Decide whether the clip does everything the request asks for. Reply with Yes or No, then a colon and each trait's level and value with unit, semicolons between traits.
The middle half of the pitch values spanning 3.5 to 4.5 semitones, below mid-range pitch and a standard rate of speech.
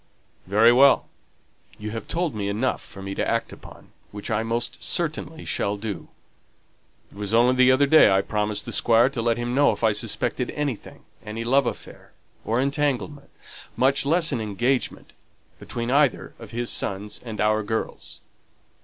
Yes: average, 4.2 semitones; low, 115 Hz; average, 170 wpm